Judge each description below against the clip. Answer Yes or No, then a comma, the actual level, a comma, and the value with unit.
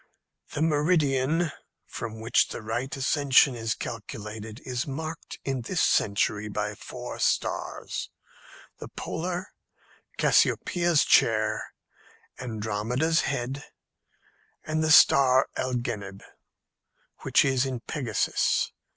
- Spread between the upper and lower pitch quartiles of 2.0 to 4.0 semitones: No, average, 5.1 semitones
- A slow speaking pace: Yes, slow, 100 wpm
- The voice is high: No, low, 130 Hz